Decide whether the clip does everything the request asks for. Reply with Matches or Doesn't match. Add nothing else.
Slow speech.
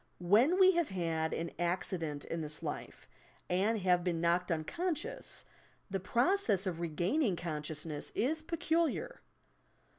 Matches